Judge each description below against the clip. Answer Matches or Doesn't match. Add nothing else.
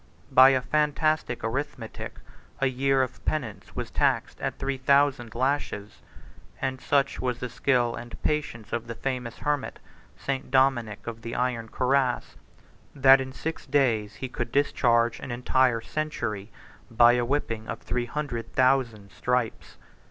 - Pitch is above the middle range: Doesn't match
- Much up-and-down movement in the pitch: Doesn't match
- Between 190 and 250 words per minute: Doesn't match